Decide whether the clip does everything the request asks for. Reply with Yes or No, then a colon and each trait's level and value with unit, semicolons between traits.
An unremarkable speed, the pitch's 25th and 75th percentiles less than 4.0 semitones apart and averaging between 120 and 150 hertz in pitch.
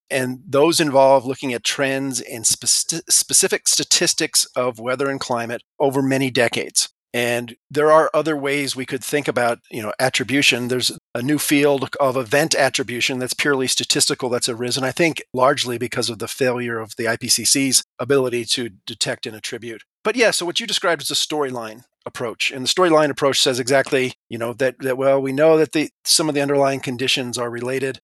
Yes: average, 190 wpm; average, 2.9 semitones; low, 135 Hz